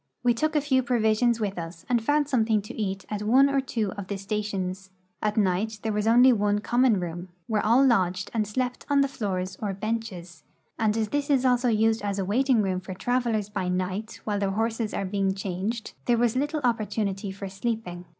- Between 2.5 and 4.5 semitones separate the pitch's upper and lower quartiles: Yes, average, 3.7 semitones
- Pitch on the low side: No, high, 215 Hz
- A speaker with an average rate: No, fast, 210 wpm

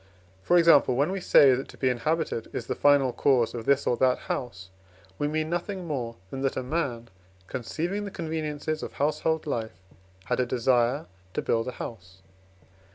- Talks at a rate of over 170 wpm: Yes, average, 180 wpm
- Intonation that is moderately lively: Yes, average, 4.7 semitones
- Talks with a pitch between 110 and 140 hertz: Yes, low, 135 Hz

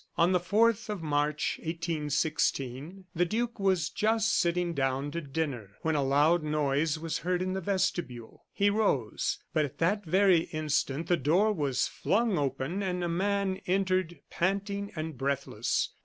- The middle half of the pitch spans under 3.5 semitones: No, average, 4.6 semitones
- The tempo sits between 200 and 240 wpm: No, average, 155 wpm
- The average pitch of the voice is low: No, medium, 170 Hz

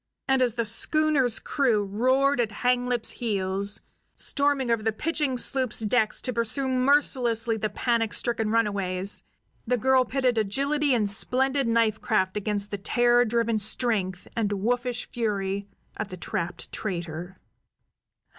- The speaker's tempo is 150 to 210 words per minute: No, average, 140 wpm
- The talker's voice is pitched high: Yes, high, 230 Hz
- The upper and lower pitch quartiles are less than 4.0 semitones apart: Yes, average, 3.5 semitones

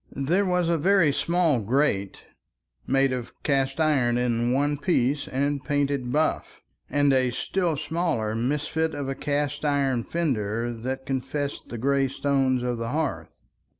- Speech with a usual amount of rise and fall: Yes, average, 3.2 semitones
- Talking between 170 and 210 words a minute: No, average, 150 wpm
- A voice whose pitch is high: No, medium, 140 Hz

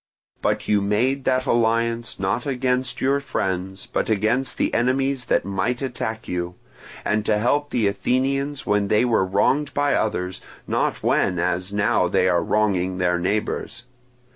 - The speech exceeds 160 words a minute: No, average, 155 wpm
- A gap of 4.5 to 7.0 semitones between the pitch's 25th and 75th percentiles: Yes, average, 5.1 semitones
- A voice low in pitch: Yes, low, 110 Hz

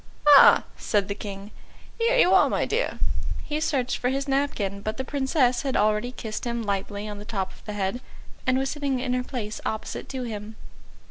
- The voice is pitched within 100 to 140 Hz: No, high, 245 Hz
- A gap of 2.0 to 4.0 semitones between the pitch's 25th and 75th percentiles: No, average, 4.6 semitones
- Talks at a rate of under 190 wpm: No, average, 200 wpm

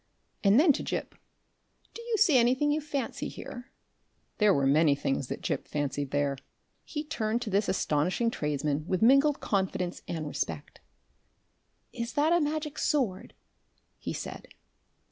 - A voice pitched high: Yes, high, 215 Hz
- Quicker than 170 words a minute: No, average, 145 wpm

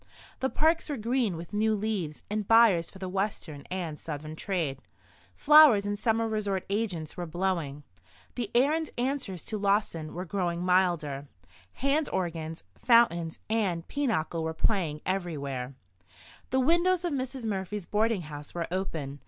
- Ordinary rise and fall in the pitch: No, wide, 5.7 semitones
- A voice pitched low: No, high, 190 Hz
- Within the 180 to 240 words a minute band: No, average, 150 wpm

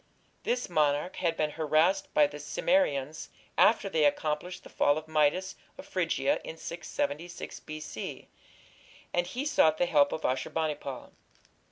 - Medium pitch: Yes, medium, 155 Hz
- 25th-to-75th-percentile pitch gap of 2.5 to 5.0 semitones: Yes, average, 3.8 semitones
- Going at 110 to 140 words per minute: No, average, 150 wpm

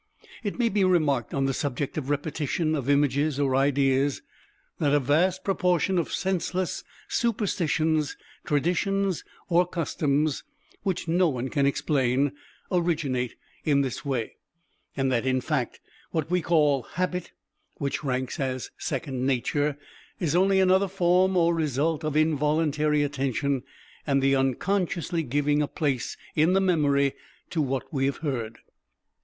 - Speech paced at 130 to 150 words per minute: Yes, average, 140 wpm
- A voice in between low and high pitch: Yes, medium, 150 Hz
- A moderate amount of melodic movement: Yes, average, 4.1 semitones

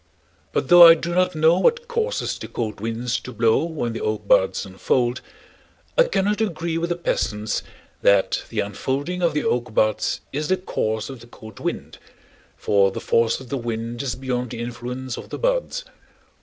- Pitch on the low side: Yes, low, 125 Hz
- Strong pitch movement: Yes, wide, 7.1 semitones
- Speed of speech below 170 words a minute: No, average, 185 wpm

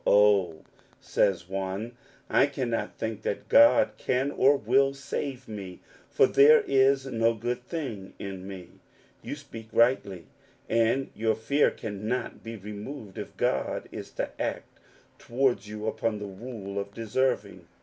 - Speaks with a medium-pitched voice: No, low, 115 Hz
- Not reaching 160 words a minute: Yes, average, 150 wpm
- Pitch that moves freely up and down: No, average, 4.7 semitones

